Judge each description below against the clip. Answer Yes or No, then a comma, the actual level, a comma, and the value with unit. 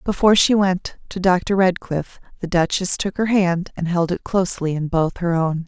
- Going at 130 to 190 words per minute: No, average, 200 wpm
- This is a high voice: No, medium, 180 Hz